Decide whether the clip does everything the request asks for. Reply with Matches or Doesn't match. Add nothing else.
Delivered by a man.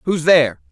Matches